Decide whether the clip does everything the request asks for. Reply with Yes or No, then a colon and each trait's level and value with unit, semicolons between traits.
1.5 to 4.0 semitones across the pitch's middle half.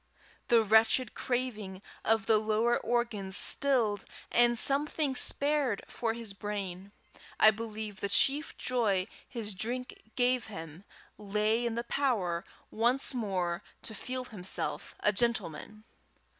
Yes: average, 3.3 semitones